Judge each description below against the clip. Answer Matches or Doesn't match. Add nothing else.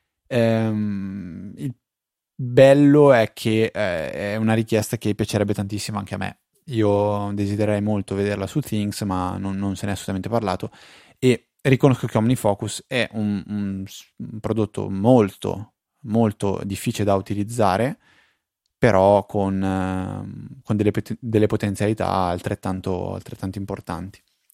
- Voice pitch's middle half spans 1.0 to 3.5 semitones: Matches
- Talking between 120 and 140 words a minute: Matches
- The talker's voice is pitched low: Matches